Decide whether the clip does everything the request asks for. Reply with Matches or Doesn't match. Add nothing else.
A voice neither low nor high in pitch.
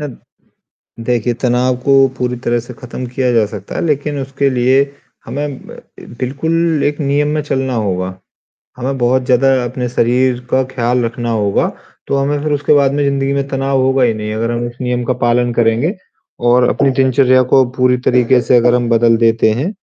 Doesn't match